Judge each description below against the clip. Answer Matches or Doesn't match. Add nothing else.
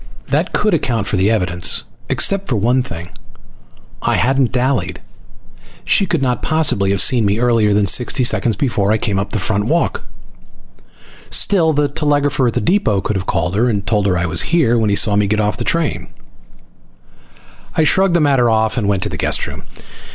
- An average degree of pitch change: Doesn't match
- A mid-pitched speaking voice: Doesn't match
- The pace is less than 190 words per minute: Doesn't match